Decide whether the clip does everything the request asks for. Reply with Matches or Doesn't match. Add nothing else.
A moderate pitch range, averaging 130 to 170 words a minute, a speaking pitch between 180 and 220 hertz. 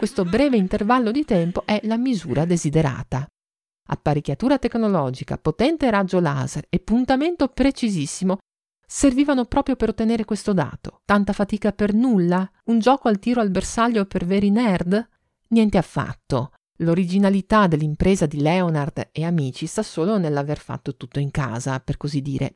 Doesn't match